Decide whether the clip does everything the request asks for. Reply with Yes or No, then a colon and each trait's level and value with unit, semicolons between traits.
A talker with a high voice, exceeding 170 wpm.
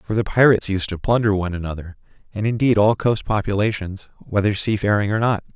No: low, 105 Hz; average, 185 wpm